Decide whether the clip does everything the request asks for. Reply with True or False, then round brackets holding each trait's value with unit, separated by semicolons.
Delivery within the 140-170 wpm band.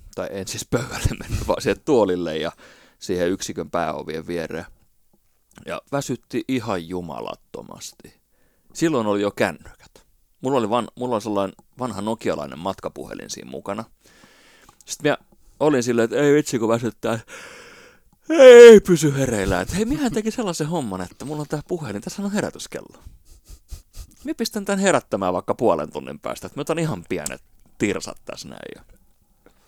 True (150 wpm)